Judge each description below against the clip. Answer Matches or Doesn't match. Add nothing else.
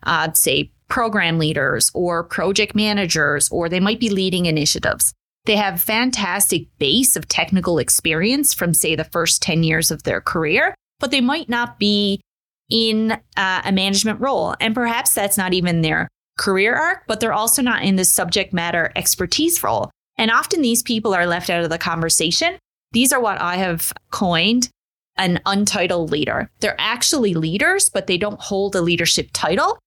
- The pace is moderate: Matches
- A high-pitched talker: Matches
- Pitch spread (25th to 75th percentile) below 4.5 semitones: Doesn't match